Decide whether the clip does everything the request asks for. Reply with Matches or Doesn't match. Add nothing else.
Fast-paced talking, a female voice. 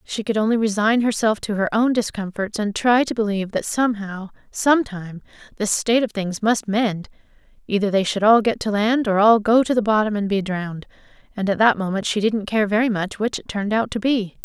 Matches